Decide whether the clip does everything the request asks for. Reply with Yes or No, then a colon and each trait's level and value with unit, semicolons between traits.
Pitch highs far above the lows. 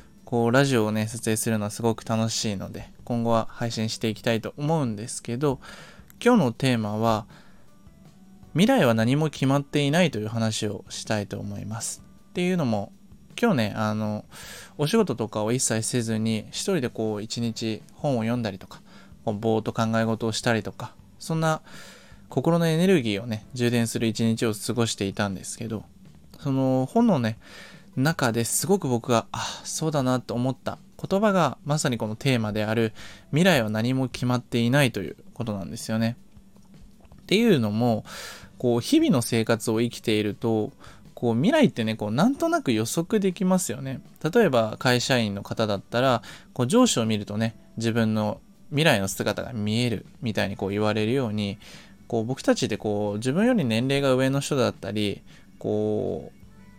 No: average, 4.2 semitones